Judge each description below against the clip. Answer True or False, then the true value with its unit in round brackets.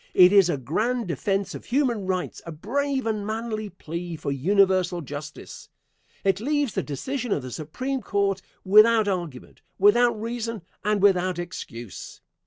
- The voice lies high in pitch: True (195 Hz)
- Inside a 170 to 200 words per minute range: False (150 wpm)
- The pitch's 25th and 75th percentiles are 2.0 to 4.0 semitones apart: False (4.8 semitones)